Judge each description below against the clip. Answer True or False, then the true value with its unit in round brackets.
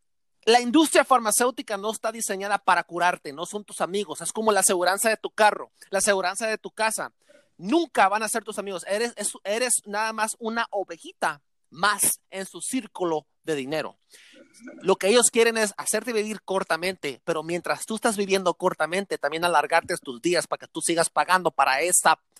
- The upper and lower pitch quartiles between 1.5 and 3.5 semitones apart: False (4.3 semitones)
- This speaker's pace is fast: False (180 wpm)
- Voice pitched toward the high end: True (200 Hz)